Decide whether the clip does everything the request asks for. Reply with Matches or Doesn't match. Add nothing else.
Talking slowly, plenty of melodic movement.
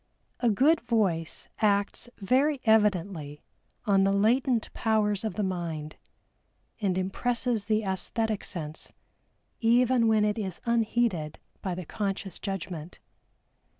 Doesn't match